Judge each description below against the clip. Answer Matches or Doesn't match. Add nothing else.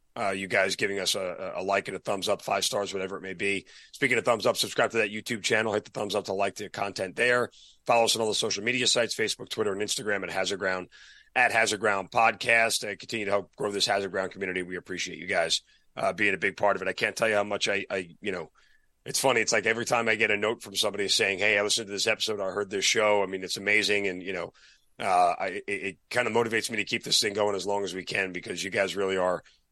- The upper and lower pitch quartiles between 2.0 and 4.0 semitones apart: Matches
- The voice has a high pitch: Doesn't match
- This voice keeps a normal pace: Doesn't match